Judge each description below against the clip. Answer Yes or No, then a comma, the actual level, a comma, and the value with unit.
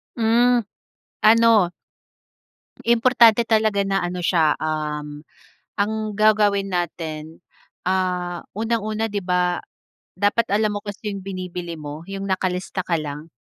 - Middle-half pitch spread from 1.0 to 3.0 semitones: No, average, 3.7 semitones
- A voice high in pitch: Yes, high, 195 Hz